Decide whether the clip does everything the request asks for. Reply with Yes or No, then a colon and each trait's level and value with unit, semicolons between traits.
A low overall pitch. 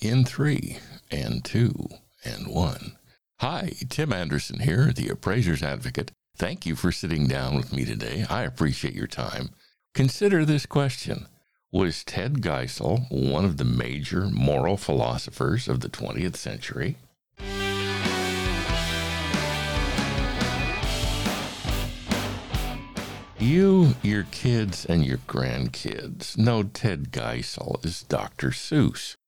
Yes: very low, 95 Hz